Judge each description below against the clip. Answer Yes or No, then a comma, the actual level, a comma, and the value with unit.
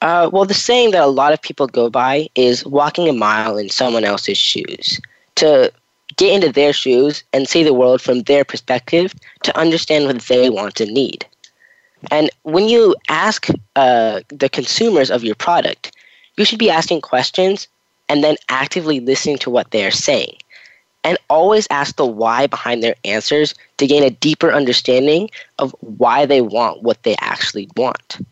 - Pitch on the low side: No, medium, 145 Hz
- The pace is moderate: Yes, average, 175 wpm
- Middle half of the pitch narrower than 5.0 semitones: No, wide, 5.5 semitones